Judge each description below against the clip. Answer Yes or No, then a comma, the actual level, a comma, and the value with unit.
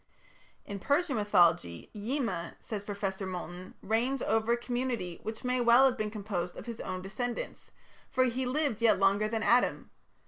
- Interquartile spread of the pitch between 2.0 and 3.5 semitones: No, average, 4.2 semitones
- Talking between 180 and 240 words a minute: No, average, 165 wpm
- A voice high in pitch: Yes, high, 220 Hz